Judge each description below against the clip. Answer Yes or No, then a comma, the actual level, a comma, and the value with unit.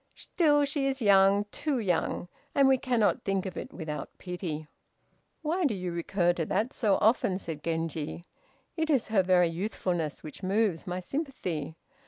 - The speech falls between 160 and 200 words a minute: Yes, average, 165 wpm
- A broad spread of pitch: Yes, wide, 6.8 semitones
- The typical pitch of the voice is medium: No, high, 195 Hz